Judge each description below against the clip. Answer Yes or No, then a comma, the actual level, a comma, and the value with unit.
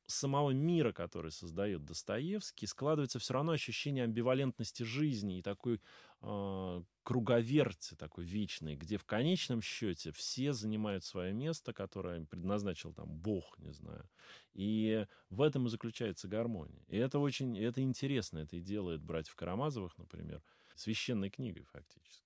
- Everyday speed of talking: Yes, average, 140 wpm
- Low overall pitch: Yes, low, 110 Hz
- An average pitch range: No, wide, 5.8 semitones